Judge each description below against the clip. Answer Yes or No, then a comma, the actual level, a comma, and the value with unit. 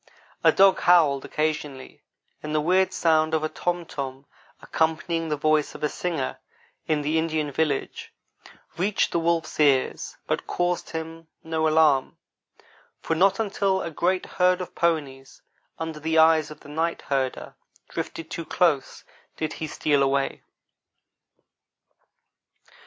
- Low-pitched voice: No, medium, 160 Hz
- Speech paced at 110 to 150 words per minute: Yes, average, 140 wpm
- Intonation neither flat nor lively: No, narrow, 2.2 semitones